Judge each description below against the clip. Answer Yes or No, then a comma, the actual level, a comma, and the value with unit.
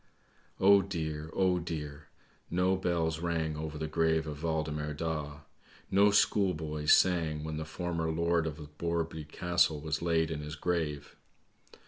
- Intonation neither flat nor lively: No, narrow, 2.1 semitones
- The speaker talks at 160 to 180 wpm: No, average, 140 wpm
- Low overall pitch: Yes, very low, 80 Hz